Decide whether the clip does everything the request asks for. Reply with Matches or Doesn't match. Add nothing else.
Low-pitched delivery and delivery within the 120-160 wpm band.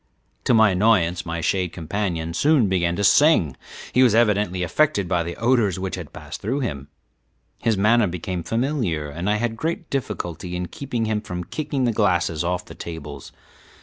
Doesn't match